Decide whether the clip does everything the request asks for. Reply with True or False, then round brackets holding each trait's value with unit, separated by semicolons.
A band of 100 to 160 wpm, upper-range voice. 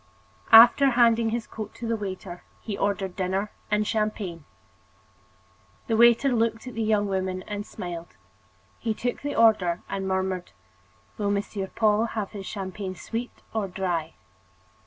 True (145 wpm; 210 Hz)